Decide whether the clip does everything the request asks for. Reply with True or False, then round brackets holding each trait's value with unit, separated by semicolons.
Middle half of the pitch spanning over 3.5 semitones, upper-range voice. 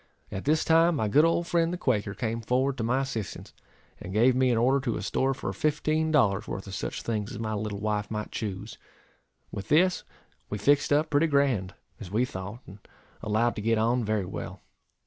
False (5.2 semitones; 115 Hz)